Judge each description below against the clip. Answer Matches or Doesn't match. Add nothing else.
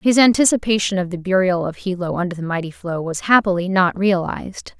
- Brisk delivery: Doesn't match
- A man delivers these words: Doesn't match